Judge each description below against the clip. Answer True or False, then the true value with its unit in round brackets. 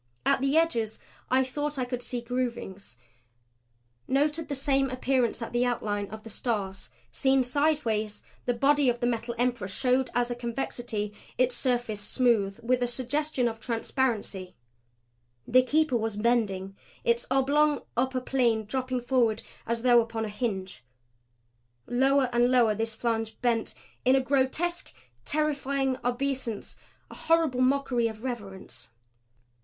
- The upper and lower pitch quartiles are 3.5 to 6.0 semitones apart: False (2.9 semitones)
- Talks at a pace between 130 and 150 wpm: True (140 wpm)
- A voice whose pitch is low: False (245 Hz)